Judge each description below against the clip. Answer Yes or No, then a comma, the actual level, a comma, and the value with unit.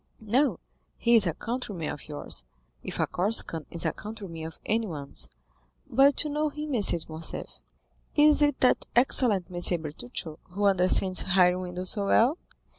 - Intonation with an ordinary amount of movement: No, wide, 6.1 semitones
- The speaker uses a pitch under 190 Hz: No, high, 195 Hz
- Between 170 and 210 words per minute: No, average, 160 wpm